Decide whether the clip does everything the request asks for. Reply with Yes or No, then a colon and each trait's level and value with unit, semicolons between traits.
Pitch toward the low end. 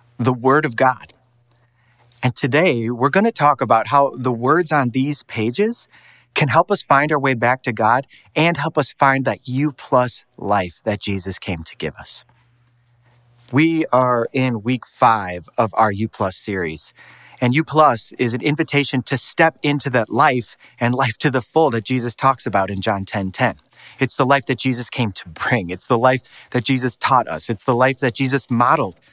Yes: low, 125 Hz